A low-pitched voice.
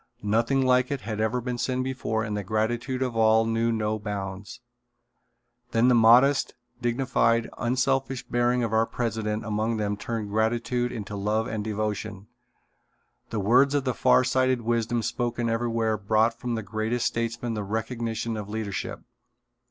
Yes: low, 115 Hz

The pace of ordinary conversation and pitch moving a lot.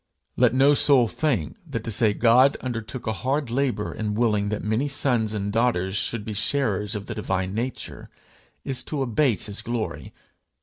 No: average, 175 wpm; average, 3.8 semitones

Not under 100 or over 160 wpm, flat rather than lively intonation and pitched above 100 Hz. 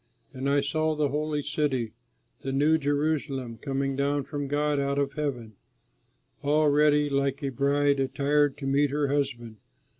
Yes: average, 155 wpm; narrow, 1.4 semitones; medium, 140 Hz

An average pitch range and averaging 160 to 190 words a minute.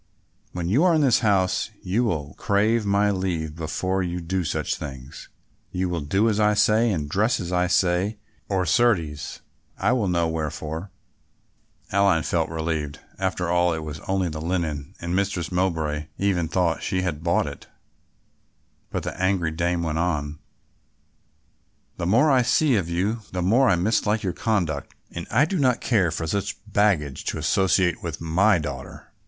Yes: average, 3.9 semitones; average, 170 wpm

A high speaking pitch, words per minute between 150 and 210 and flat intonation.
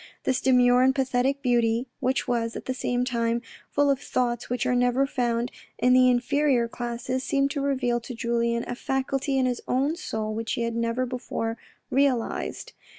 Yes: very high, 250 Hz; average, 180 wpm; narrow, 2.0 semitones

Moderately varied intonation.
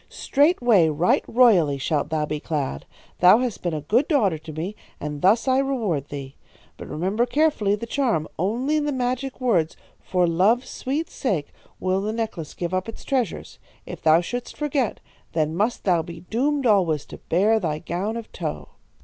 No: wide, 7.4 semitones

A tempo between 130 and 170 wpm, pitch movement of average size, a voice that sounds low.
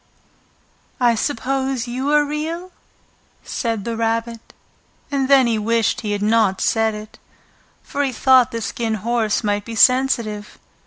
No: average, 145 wpm; average, 3.2 semitones; high, 230 Hz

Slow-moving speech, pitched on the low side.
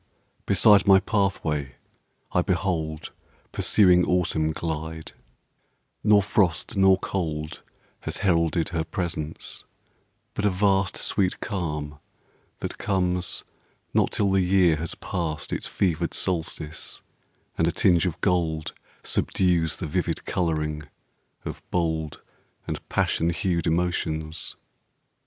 Yes: slow, 115 wpm; very low, 85 Hz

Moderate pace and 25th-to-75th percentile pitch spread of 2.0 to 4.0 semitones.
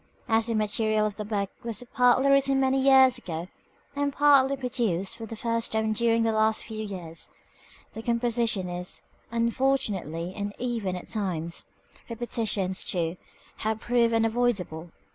Yes: average, 145 wpm; average, 3.5 semitones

